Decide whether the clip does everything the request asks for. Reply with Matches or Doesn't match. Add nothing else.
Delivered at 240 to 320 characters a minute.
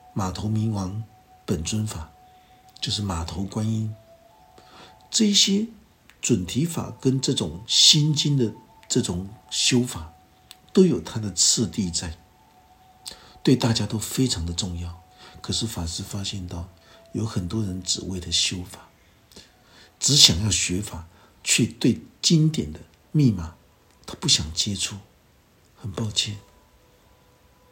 Doesn't match